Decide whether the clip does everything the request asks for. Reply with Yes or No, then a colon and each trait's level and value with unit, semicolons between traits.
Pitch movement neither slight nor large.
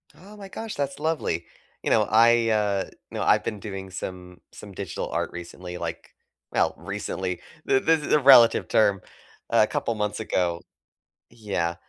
Yes: average, 4.8 semitones